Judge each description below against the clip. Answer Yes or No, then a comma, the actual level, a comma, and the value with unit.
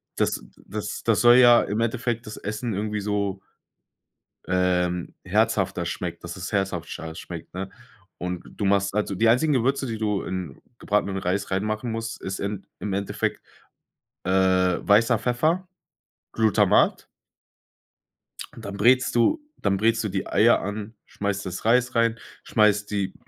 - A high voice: No, low, 105 Hz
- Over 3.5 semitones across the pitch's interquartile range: No, average, 3.2 semitones